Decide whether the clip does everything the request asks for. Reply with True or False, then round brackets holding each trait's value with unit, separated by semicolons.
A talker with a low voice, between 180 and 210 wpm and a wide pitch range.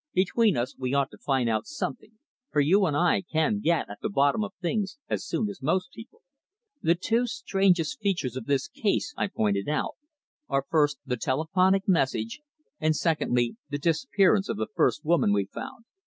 False (165 Hz; 185 wpm; 6.3 semitones)